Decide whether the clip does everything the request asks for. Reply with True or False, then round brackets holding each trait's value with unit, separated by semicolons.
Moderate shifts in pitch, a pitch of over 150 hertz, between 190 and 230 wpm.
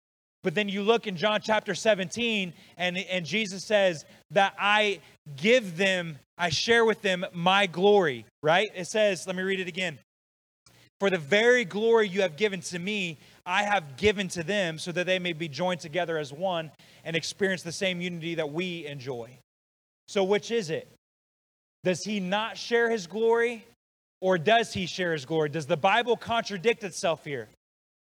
False (3.9 semitones; 185 Hz; 175 wpm)